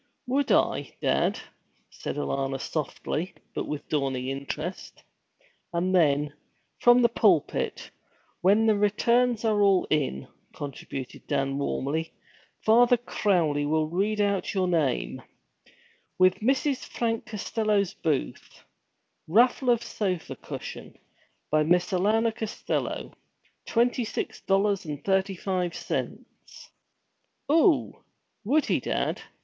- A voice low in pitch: No, high, 190 Hz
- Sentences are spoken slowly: Yes, slow, 110 wpm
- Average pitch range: No, wide, 6.4 semitones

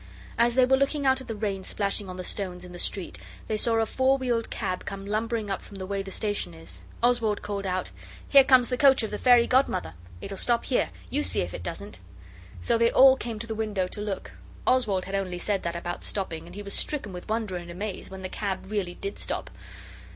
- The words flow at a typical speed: No, fast, 235 wpm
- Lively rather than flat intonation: No, average, 4.2 semitones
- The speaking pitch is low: No, high, 205 Hz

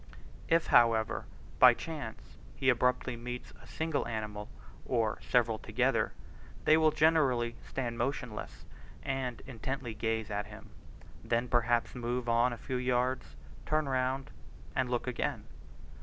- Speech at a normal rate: No, slow, 130 wpm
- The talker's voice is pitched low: Yes, low, 125 Hz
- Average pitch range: No, narrow, 2.3 semitones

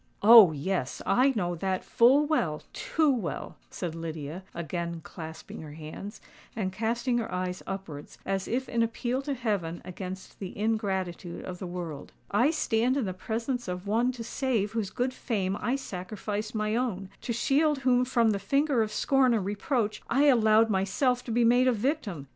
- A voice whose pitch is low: No, high, 215 Hz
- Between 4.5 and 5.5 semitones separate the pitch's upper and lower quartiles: Yes, average, 5.1 semitones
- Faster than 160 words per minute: Yes, average, 170 wpm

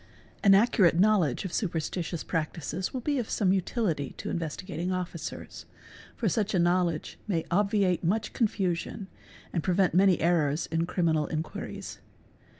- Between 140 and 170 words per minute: Yes, average, 150 wpm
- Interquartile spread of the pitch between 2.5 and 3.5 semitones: Yes, average, 3.2 semitones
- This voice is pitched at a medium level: Yes, medium, 180 Hz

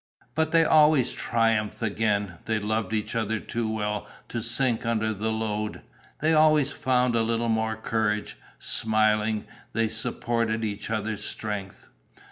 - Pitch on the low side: Yes, low, 110 Hz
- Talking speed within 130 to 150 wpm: Yes, average, 140 wpm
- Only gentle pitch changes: Yes, narrow, 1.5 semitones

